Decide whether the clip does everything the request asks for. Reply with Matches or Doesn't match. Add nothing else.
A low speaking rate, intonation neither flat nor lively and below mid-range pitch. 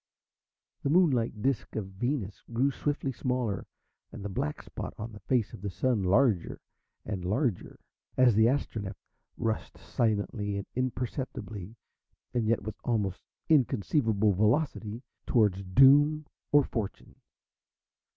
Matches